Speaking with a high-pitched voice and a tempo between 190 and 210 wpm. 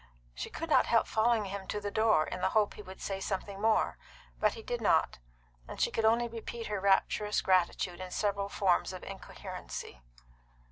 Yes: high, 205 Hz; average, 195 wpm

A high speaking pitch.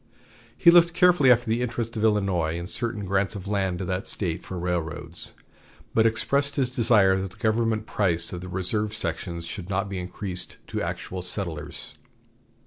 No: low, 100 Hz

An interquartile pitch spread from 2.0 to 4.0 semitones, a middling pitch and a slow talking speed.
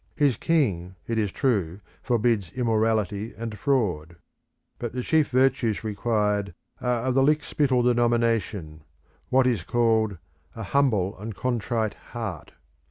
No: average, 3.5 semitones; low, 115 Hz; slow, 130 wpm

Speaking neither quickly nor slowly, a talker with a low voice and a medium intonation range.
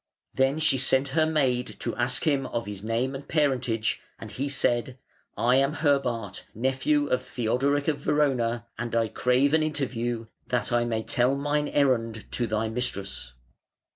Yes: average, 165 wpm; low, 125 Hz; average, 3.3 semitones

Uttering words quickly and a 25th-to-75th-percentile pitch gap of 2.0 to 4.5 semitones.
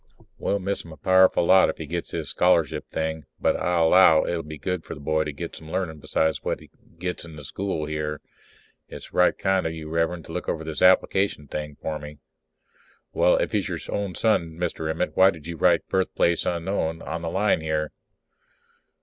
Yes: fast, 210 wpm; average, 2.8 semitones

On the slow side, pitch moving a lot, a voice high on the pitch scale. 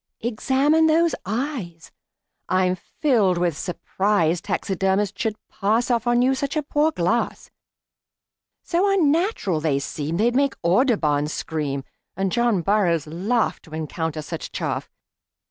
Yes: slow, 125 wpm; wide, 7.4 semitones; high, 205 Hz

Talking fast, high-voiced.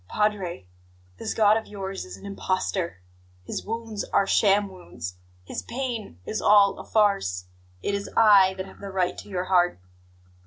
No: average, 165 wpm; high, 195 Hz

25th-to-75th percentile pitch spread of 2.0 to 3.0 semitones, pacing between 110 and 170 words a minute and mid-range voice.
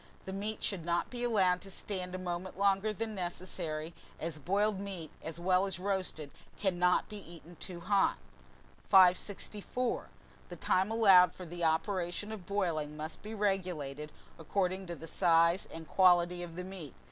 Yes: narrow, 2.6 semitones; average, 160 wpm; medium, 180 Hz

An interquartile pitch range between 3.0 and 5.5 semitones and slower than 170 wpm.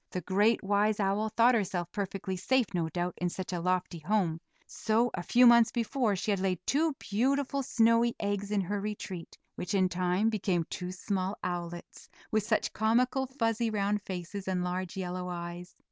No: average, 3.7 semitones; average, 175 wpm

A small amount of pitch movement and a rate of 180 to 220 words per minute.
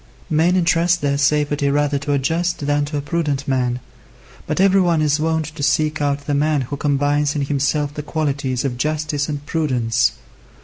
Yes: narrow, 1.7 semitones; average, 185 wpm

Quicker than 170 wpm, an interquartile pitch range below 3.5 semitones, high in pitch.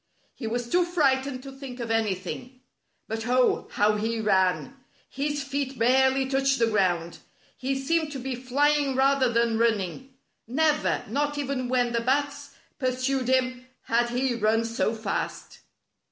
No: average, 160 wpm; average, 2.9 semitones; very high, 255 Hz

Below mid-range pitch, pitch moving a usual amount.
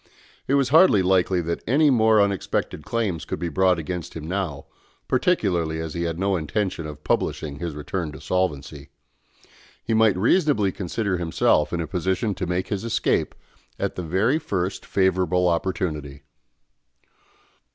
Yes: very low, 90 Hz; average, 3.9 semitones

